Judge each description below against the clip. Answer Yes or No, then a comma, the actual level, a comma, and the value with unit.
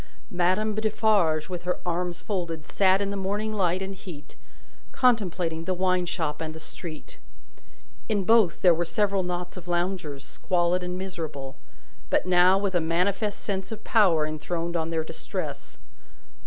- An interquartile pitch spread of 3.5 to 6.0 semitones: No, average, 2.7 semitones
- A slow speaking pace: No, average, 155 wpm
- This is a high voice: No, medium, 180 Hz